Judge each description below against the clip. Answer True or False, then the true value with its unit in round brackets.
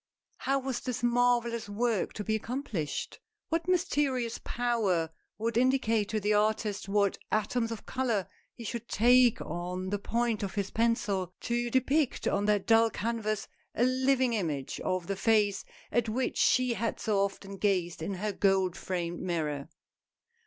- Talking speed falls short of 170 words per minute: True (155 wpm)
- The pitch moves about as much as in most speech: True (3.5 semitones)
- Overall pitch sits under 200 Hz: False (220 Hz)